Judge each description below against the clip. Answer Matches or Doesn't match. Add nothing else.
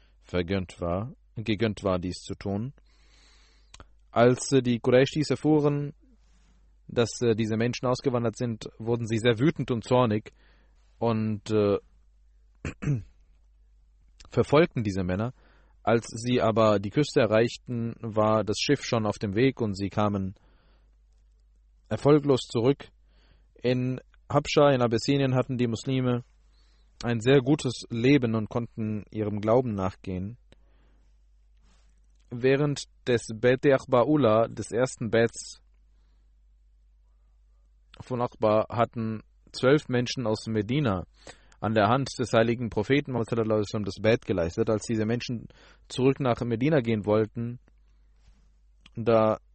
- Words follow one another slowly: Matches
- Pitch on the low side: Matches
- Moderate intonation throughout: Matches